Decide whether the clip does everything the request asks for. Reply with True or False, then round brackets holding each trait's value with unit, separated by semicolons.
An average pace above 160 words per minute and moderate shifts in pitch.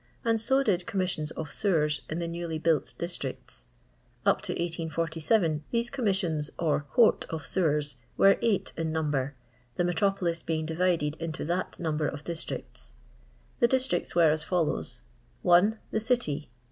False (155 wpm; 3.6 semitones)